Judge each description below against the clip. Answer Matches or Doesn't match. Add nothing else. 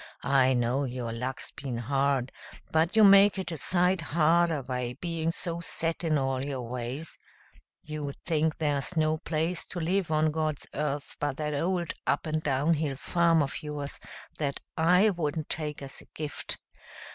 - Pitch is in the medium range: Matches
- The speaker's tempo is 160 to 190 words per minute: Matches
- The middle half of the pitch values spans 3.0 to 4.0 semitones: Matches